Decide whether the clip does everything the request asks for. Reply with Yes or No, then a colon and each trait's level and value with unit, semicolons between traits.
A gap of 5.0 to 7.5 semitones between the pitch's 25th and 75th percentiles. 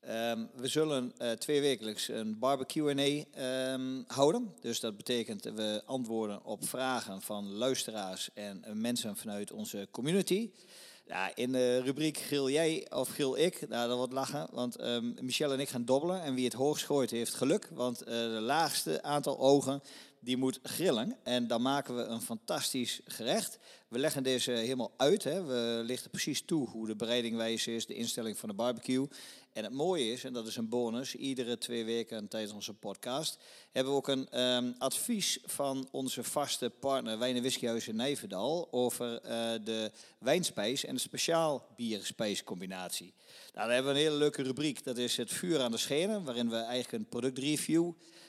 No: average, 3.2 semitones